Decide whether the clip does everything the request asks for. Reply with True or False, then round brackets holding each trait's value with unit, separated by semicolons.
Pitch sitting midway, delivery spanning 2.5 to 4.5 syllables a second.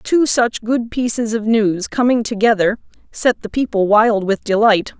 False (220 Hz; 4.4 syllables/s)